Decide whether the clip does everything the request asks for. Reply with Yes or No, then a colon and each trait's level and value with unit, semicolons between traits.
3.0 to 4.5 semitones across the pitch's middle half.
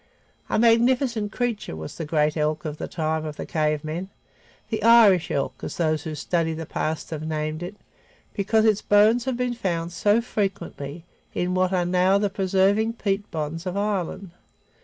No: average, 5.0 semitones